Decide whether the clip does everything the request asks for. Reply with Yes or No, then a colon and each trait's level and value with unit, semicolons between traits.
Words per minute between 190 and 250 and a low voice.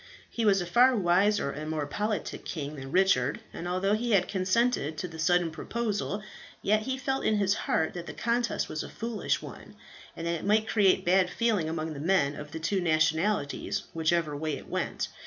No: average, 200 wpm; medium, 180 Hz